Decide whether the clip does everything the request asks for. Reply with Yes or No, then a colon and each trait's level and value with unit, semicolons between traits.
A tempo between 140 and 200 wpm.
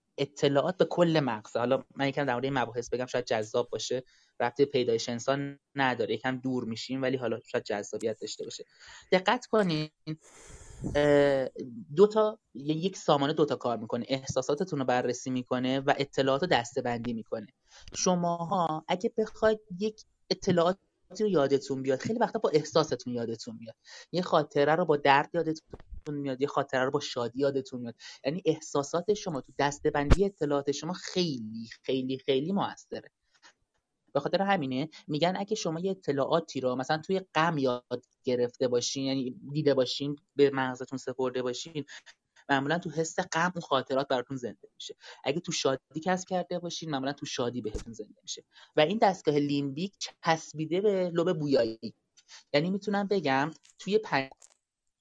Yes: fast, 155 wpm